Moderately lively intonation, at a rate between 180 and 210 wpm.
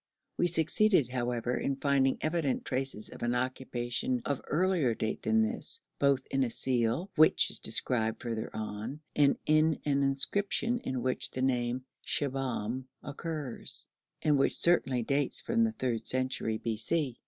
No: average, 4.1 semitones; average, 150 wpm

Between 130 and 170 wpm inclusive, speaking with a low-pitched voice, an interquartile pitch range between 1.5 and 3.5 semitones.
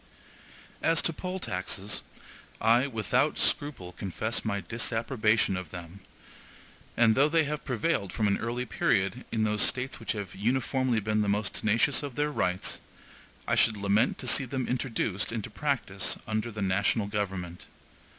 No: average, 155 wpm; low, 110 Hz; average, 4.2 semitones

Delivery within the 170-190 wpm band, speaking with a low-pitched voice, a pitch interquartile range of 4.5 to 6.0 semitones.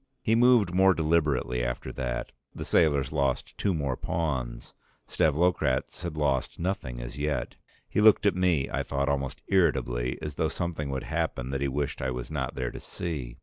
Yes: average, 180 wpm; very low, 75 Hz; average, 4.8 semitones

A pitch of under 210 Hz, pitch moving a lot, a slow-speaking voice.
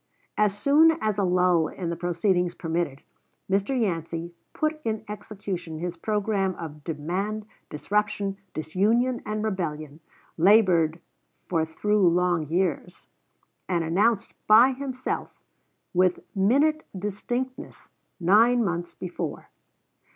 No: high, 190 Hz; average, 4.0 semitones; slow, 110 wpm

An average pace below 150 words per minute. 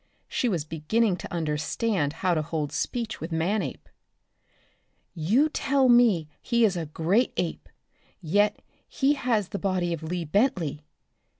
Yes: average, 140 wpm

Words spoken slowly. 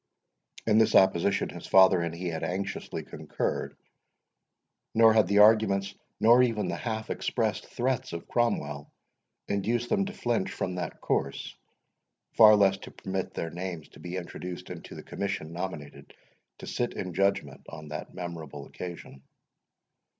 No: average, 150 wpm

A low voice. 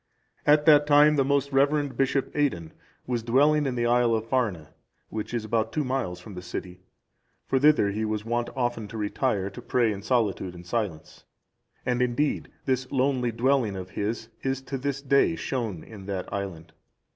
Yes: low, 120 Hz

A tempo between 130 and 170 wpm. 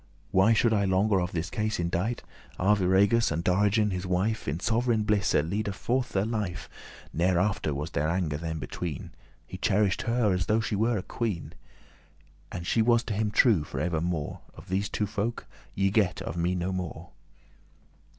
No: average, 180 wpm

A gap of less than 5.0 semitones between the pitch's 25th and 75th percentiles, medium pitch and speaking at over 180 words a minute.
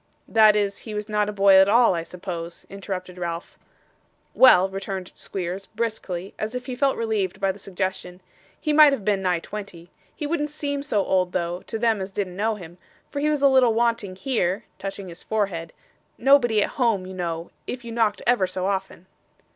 No: average, 3.9 semitones; high, 200 Hz; average, 195 wpm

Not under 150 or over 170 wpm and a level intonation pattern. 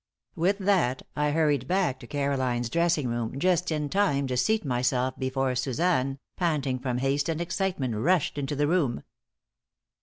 No: average, 155 wpm; average, 4.9 semitones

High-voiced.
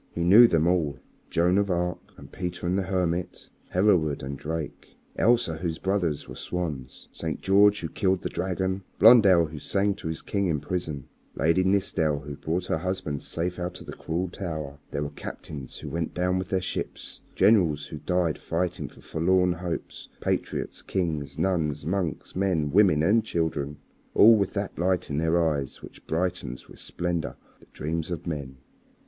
No: very low, 85 Hz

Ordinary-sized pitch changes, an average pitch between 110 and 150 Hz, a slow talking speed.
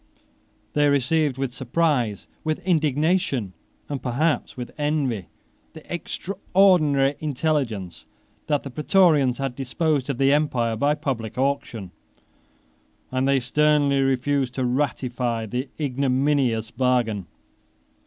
Yes: average, 3.3 semitones; low, 135 Hz; slow, 110 wpm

